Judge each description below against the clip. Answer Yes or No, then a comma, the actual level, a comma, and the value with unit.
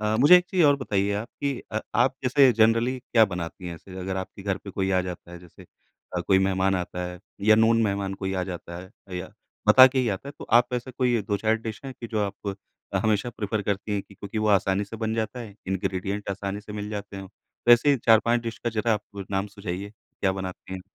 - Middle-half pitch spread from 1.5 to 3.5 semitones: Yes, average, 3.2 semitones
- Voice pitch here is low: Yes, low, 105 Hz